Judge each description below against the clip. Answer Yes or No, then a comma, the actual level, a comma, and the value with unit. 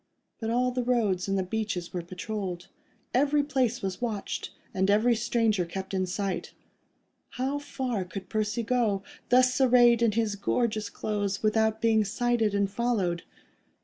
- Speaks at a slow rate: No, average, 150 wpm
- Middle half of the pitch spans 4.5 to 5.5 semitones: No, average, 3.6 semitones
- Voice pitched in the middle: No, high, 220 Hz